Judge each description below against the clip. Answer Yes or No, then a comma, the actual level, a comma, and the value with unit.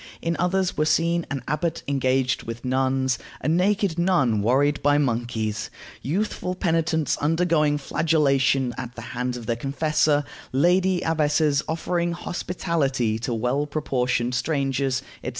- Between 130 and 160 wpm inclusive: Yes, slow, 135 wpm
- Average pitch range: Yes, average, 4.6 semitones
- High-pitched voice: No, medium, 145 Hz